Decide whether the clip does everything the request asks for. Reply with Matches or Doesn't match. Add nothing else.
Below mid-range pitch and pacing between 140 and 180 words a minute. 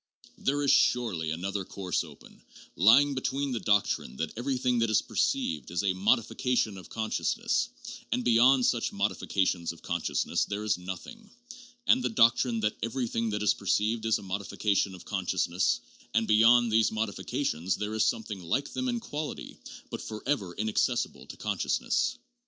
Matches